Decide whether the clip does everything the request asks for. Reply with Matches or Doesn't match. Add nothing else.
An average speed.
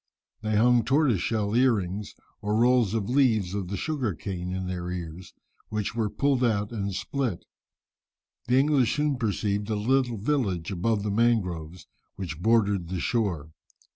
Matches